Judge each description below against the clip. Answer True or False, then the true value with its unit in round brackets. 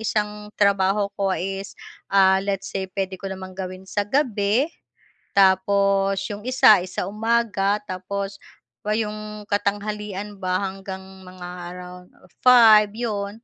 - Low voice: False (200 Hz)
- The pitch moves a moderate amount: False (1.7 semitones)